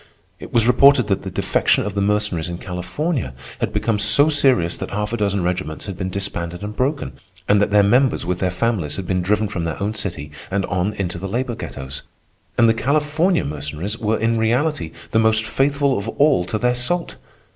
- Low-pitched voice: Yes, low, 105 Hz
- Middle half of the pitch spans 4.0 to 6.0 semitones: Yes, average, 5.2 semitones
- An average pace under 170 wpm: No, fast, 205 wpm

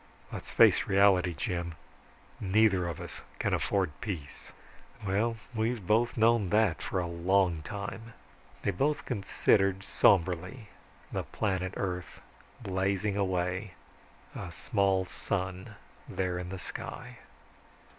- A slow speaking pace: Yes, slow, 115 wpm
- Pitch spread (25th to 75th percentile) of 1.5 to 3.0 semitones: Yes, narrow, 2.4 semitones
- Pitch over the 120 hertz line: No, very low, 95 Hz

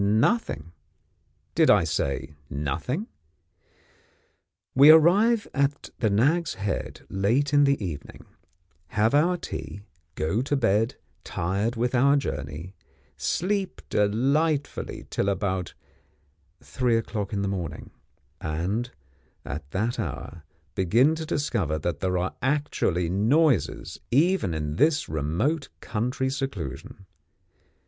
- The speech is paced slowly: Yes, slow, 110 wpm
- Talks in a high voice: No, low, 115 Hz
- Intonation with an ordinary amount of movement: No, wide, 7.9 semitones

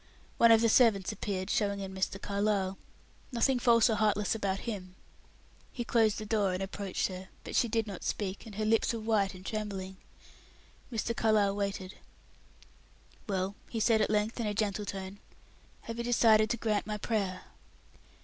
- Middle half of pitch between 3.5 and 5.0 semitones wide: No, narrow, 2.4 semitones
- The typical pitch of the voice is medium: No, high, 210 Hz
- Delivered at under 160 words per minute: No, average, 175 wpm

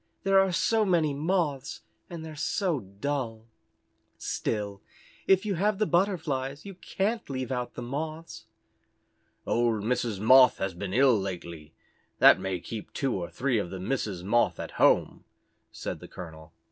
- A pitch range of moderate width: No, wide, 8.3 semitones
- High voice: No, low, 130 Hz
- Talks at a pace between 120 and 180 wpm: Yes, average, 155 wpm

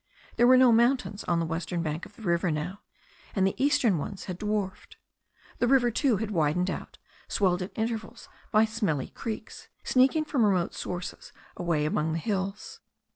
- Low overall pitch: No, high, 195 Hz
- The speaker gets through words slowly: No, average, 175 wpm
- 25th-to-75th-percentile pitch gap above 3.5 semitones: Yes, average, 4.9 semitones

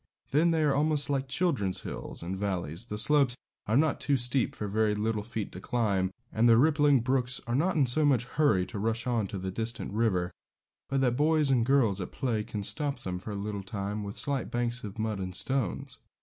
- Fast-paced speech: Yes, fast, 220 wpm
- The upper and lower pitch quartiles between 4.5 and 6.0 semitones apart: Yes, average, 5.1 semitones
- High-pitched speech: No, low, 115 Hz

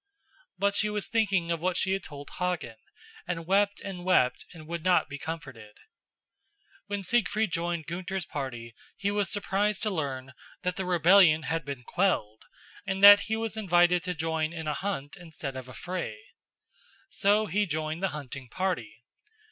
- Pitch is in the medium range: Yes, medium, 175 Hz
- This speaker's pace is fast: No, average, 170 wpm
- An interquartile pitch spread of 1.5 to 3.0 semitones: No, average, 4.1 semitones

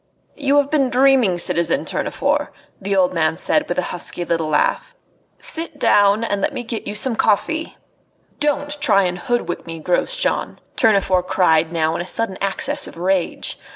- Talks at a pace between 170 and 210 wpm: Yes, average, 175 wpm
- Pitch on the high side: Yes, high, 200 Hz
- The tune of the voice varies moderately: No, wide, 7.4 semitones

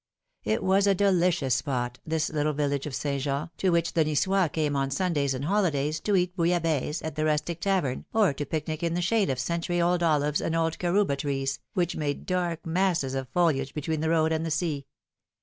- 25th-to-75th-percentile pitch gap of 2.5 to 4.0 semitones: Yes, average, 3.6 semitones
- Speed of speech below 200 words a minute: No, fast, 205 wpm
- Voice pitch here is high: No, medium, 160 Hz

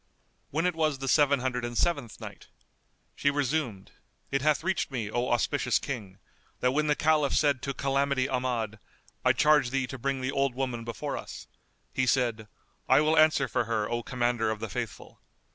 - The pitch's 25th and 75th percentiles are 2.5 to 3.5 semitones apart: Yes, average, 3.1 semitones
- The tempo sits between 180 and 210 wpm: Yes, average, 185 wpm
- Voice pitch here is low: Yes, low, 130 Hz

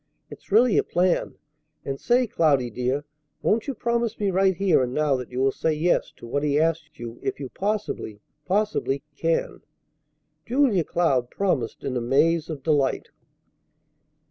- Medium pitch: Yes, medium, 160 Hz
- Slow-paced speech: No, average, 165 wpm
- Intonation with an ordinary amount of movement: No, wide, 6.6 semitones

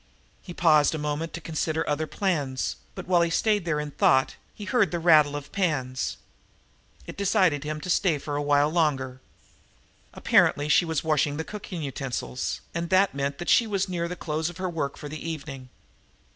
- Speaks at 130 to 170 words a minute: No, average, 185 wpm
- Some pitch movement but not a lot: Yes, average, 3.3 semitones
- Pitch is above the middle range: No, medium, 155 Hz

